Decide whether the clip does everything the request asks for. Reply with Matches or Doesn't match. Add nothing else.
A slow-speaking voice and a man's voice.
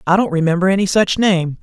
Doesn't match